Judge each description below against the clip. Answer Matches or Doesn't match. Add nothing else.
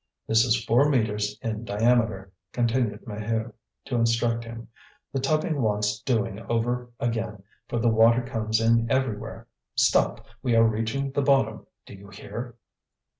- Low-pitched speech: Matches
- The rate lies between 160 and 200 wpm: Doesn't match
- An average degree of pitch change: Doesn't match